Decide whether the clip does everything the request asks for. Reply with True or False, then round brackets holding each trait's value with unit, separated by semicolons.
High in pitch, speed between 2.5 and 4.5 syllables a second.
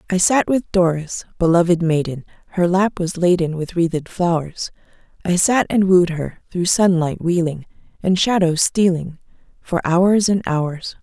False (175 Hz; 4.4 syllables/s)